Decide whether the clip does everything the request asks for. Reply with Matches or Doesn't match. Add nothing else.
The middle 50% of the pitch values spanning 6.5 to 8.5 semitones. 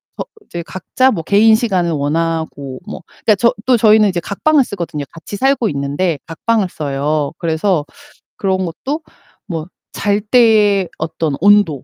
Doesn't match